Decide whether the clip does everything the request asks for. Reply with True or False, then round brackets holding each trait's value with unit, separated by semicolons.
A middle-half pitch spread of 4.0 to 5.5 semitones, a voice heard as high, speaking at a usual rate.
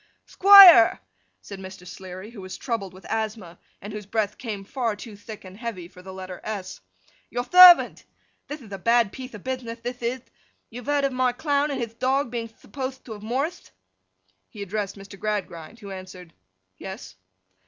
True (4.5 semitones; 220 Hz; 180 wpm)